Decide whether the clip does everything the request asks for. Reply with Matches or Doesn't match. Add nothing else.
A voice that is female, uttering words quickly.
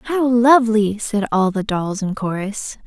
Doesn't match